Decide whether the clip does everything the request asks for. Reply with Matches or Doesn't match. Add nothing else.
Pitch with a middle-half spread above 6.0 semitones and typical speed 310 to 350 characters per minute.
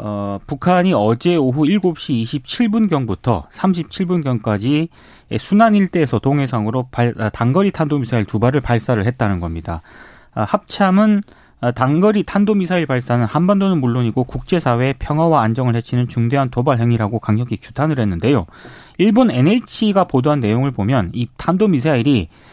Matches